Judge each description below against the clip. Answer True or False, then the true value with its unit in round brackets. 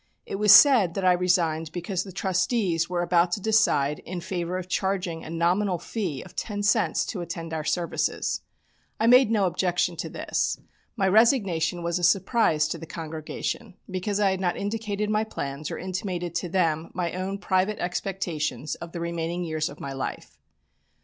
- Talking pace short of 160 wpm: False (180 wpm)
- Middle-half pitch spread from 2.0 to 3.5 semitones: True (2.9 semitones)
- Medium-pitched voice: True (180 Hz)